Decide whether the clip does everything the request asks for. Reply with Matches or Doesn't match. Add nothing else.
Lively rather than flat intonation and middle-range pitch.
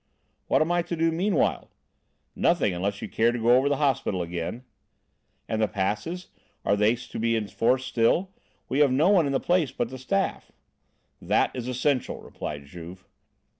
Doesn't match